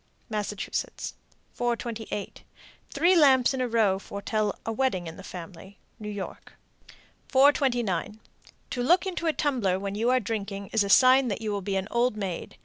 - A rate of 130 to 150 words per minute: No, average, 165 wpm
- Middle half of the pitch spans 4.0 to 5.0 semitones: Yes, average, 4.3 semitones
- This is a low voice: No, high, 220 Hz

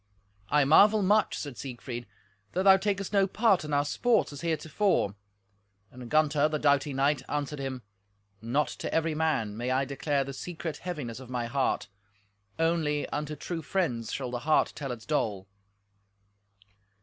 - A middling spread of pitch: Yes, average, 4.0 semitones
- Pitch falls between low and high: Yes, medium, 150 Hz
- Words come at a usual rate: Yes, average, 160 wpm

